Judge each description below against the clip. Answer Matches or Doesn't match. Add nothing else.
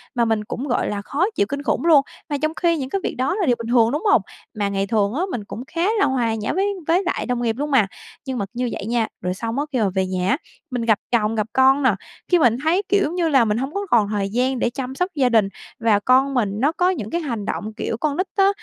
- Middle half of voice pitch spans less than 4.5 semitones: Doesn't match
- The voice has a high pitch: Matches